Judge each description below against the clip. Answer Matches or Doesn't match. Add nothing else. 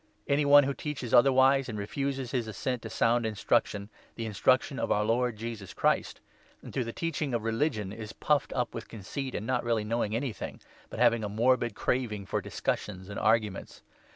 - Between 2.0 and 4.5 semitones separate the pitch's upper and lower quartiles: Matches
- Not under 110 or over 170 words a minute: Doesn't match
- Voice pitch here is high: Doesn't match